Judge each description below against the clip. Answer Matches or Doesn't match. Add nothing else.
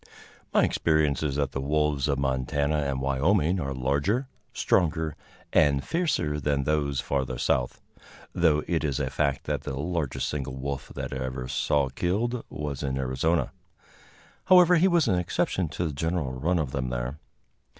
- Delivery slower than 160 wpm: Doesn't match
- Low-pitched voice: Matches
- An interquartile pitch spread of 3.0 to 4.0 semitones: Matches